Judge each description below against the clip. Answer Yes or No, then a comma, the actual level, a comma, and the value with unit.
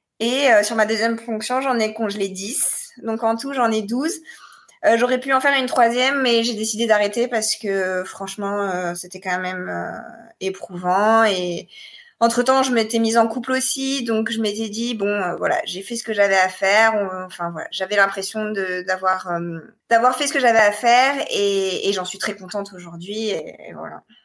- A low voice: No, high, 220 Hz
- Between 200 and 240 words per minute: Yes, average, 205 wpm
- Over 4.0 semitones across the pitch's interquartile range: No, average, 3.6 semitones